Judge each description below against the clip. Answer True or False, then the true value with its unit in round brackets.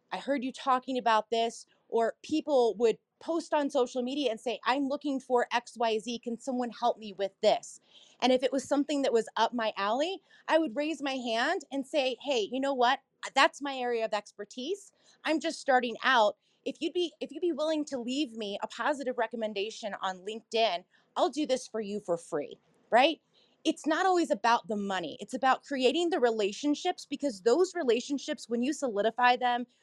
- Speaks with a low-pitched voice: False (255 Hz)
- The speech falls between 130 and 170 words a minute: False (195 wpm)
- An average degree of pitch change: True (4.4 semitones)